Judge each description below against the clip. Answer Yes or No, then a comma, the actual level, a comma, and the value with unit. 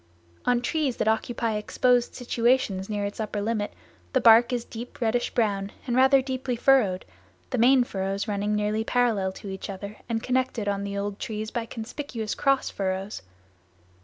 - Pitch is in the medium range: No, high, 225 Hz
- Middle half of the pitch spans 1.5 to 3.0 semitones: No, average, 3.4 semitones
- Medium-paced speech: Yes, average, 165 wpm